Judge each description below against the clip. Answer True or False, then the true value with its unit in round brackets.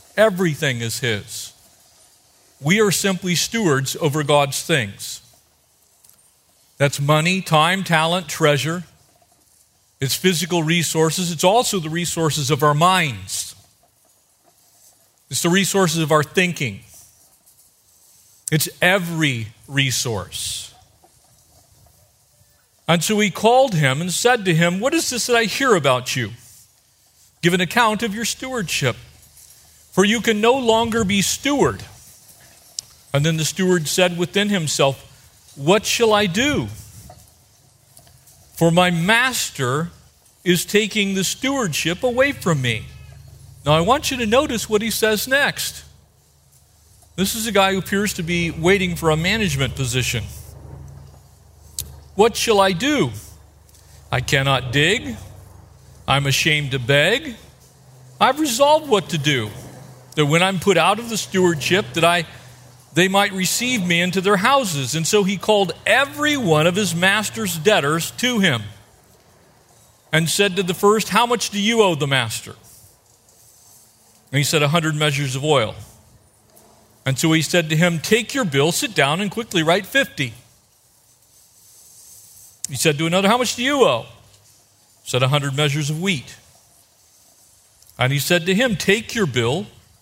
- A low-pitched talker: False (155 Hz)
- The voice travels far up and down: True (8.6 semitones)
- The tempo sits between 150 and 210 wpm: False (140 wpm)